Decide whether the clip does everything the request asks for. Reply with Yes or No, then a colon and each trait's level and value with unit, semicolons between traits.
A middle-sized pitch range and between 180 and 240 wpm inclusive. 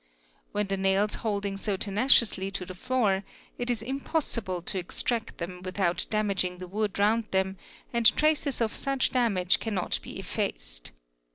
No: average, 3.7 semitones; average, 160 wpm